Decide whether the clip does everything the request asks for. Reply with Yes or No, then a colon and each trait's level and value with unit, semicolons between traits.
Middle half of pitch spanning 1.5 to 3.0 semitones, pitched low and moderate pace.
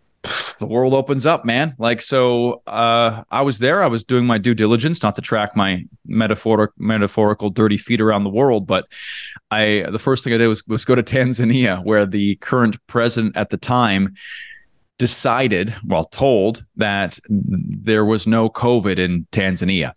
Yes: narrow, 2.6 semitones; low, 110 Hz; average, 170 wpm